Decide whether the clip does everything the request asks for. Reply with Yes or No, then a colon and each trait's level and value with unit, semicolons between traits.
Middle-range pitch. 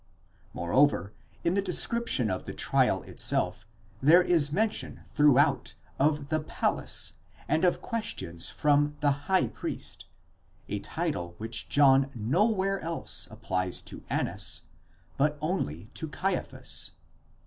Yes: medium, 145 Hz